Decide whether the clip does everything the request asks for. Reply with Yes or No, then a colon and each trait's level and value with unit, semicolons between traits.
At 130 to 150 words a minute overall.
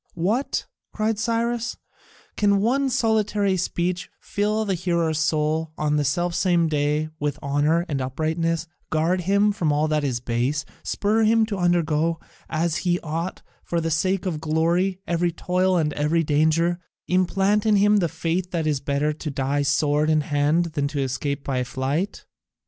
No: average, 165 wpm